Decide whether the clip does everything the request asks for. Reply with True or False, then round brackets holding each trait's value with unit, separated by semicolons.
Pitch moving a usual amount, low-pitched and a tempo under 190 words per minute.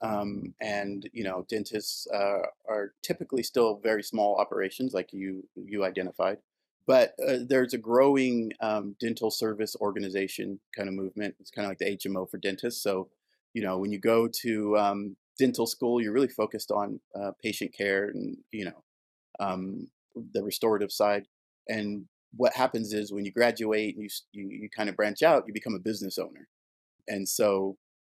False (2.3 semitones; 105 Hz; 180 wpm)